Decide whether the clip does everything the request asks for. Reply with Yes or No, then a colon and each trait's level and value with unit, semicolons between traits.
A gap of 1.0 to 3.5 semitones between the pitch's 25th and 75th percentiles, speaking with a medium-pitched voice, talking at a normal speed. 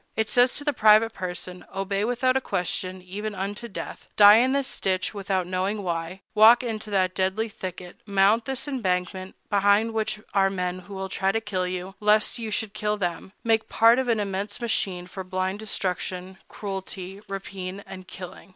No: average, 2.7 semitones; high, 195 Hz; average, 180 wpm